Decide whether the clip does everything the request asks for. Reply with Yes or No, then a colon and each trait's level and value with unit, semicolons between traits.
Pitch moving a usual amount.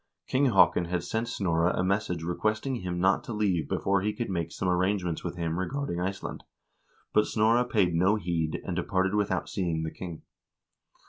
Yes: average, 3.4 semitones